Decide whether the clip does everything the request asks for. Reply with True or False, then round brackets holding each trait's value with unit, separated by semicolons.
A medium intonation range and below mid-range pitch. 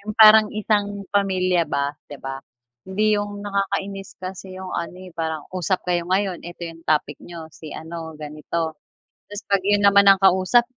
False (3.3 semitones; 185 Hz)